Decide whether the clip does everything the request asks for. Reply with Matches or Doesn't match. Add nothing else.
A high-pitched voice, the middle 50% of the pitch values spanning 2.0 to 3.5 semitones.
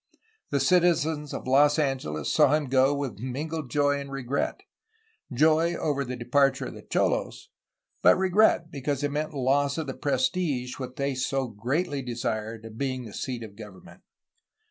Doesn't match